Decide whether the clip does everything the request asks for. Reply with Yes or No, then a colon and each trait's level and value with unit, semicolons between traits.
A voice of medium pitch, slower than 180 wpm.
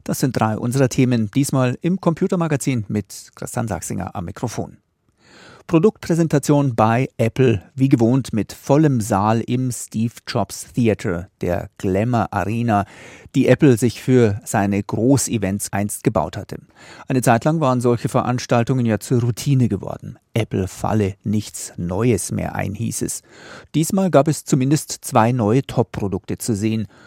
No: low, 120 Hz; average, 135 wpm